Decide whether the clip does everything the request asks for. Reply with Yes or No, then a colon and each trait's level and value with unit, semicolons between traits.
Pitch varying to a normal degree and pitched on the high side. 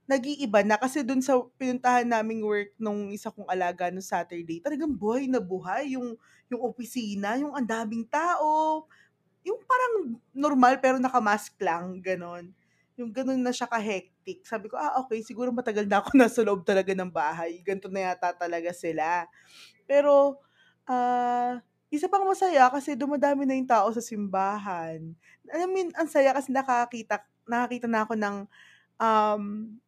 Yes: average, 4.7 semitones; high, 235 Hz